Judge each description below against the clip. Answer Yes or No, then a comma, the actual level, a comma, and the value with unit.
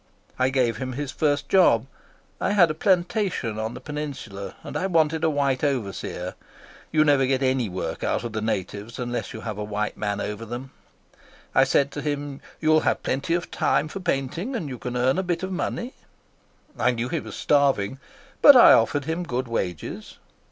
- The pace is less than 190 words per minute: No, average, 195 wpm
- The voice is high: No, low, 135 Hz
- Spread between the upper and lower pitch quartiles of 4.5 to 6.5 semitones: Yes, average, 5.2 semitones